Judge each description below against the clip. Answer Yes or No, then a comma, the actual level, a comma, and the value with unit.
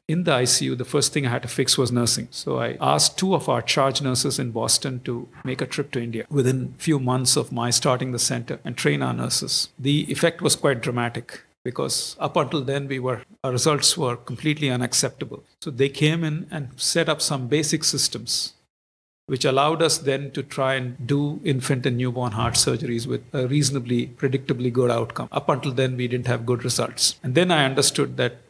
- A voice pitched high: No, low, 135 Hz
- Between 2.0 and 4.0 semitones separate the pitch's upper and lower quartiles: Yes, average, 3.0 semitones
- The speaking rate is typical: No, fast, 210 wpm